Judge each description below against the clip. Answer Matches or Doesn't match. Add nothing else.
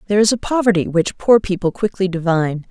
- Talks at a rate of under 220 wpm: Matches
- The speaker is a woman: Matches